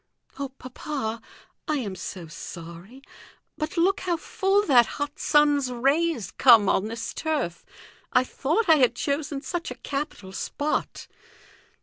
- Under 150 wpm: Yes, slow, 135 wpm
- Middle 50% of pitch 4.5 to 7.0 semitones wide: Yes, average, 5.2 semitones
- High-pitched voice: Yes, very high, 275 Hz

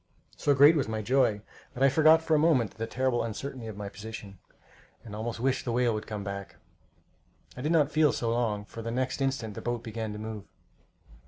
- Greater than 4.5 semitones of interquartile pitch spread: No, average, 3.8 semitones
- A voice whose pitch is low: Yes, low, 120 Hz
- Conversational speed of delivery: No, fast, 215 wpm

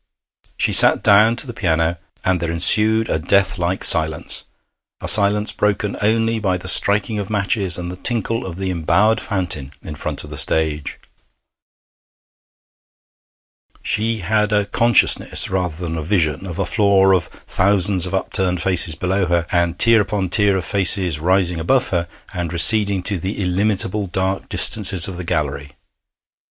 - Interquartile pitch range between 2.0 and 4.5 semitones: Yes, average, 3.2 semitones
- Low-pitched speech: Yes, very low, 95 Hz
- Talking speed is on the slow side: No, average, 160 wpm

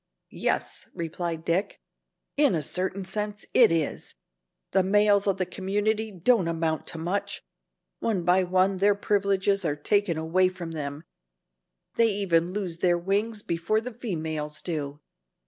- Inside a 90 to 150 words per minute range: Yes, average, 145 wpm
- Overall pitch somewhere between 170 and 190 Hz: Yes, medium, 185 Hz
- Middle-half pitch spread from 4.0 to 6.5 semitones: No, average, 3.6 semitones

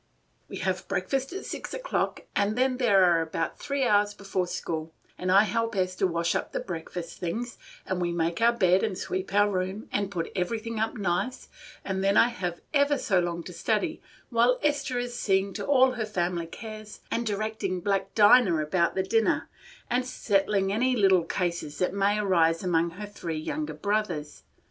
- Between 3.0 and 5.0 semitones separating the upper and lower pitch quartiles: Yes, average, 4.4 semitones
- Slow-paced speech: No, average, 185 wpm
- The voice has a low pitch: No, high, 200 Hz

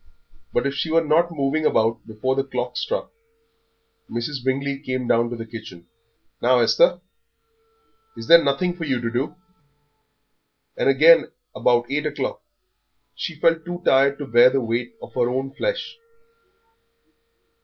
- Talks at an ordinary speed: Yes, average, 150 wpm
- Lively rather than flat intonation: No, average, 4.6 semitones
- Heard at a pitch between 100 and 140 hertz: Yes, low, 135 Hz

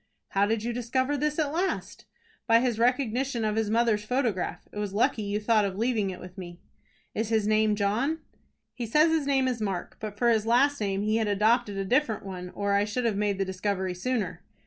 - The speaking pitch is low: No, high, 220 Hz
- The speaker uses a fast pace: Yes, fast, 215 wpm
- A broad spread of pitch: No, average, 3.4 semitones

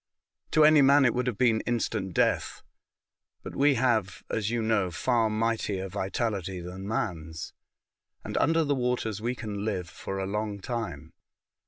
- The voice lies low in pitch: Yes, low, 110 Hz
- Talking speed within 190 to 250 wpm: No, average, 165 wpm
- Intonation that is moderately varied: Yes, average, 4.3 semitones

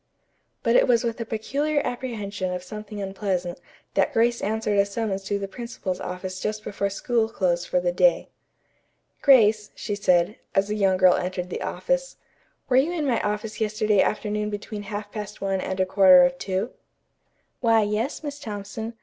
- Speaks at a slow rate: No, average, 175 wpm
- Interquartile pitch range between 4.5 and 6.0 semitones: No, average, 3.0 semitones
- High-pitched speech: Yes, high, 210 Hz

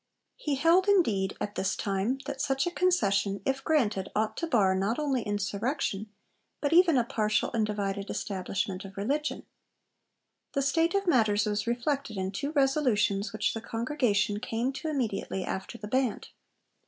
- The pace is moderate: Yes, average, 160 wpm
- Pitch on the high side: Yes, high, 225 Hz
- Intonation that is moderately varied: No, wide, 5.7 semitones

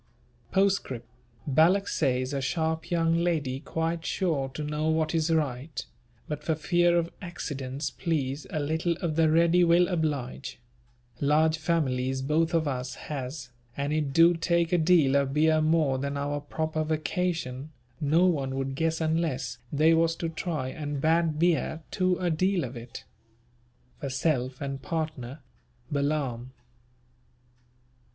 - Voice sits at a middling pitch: Yes, medium, 155 Hz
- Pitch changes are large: No, average, 3.2 semitones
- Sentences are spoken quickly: No, average, 145 wpm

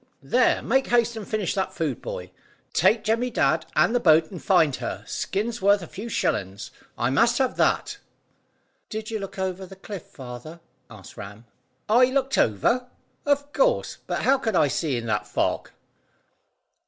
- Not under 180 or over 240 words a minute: No, average, 170 wpm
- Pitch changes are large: Yes, wide, 7.6 semitones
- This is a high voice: Yes, high, 205 Hz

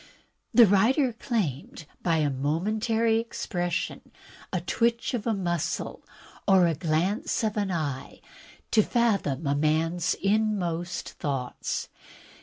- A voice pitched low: No, medium, 180 Hz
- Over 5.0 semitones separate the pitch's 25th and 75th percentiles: Yes, wide, 5.5 semitones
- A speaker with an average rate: No, slow, 115 wpm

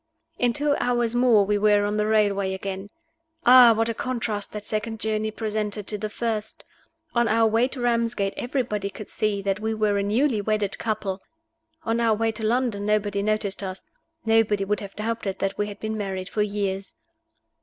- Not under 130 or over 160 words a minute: No, average, 185 wpm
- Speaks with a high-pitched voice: Yes, high, 215 Hz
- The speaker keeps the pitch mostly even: Yes, narrow, 1.9 semitones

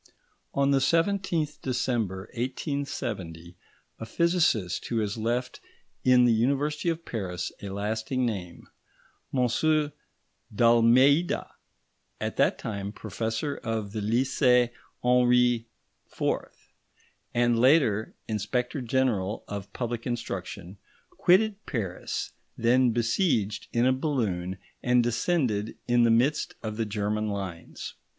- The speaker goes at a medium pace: No, slow, 110 wpm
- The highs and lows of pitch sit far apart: No, average, 3.8 semitones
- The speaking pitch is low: Yes, low, 120 Hz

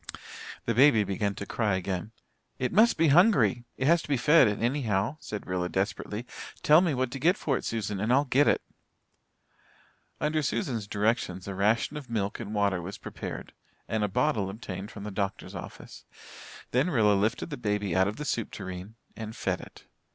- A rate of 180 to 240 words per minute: Yes, average, 190 wpm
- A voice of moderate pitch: No, low, 110 Hz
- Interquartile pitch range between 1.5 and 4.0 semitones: No, average, 5.3 semitones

